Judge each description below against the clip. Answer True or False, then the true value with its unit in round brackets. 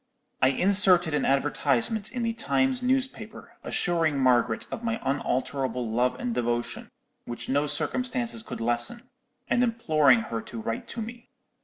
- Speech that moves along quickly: False (145 wpm)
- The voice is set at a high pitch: False (150 Hz)